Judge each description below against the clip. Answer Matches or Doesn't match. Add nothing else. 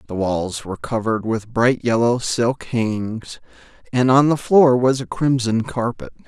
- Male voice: Matches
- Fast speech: Doesn't match